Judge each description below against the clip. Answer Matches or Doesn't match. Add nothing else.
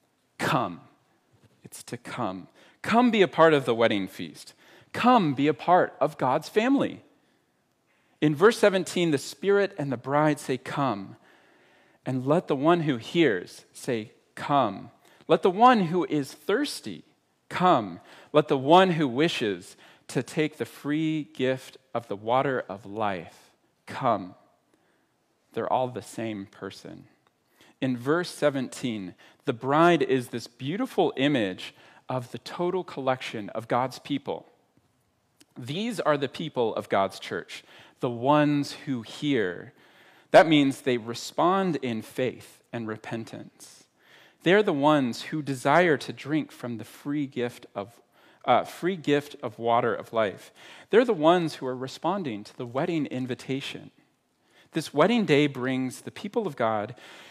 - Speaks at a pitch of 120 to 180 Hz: Matches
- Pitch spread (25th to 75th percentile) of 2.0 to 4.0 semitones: Doesn't match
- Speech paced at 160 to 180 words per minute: Doesn't match